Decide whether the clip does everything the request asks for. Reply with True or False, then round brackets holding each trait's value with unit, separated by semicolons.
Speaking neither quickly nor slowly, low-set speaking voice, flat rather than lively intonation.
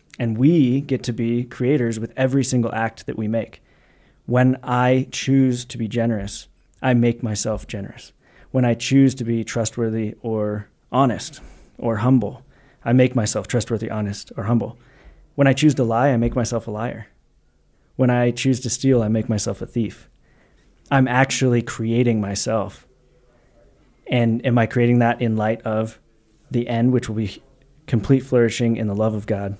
True (170 wpm; 120 Hz; 2.3 semitones)